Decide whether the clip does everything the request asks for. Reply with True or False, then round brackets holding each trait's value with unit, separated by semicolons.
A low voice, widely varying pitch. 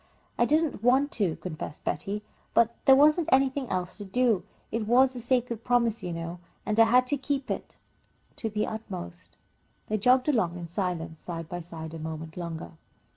False (215 Hz; 6.8 semitones)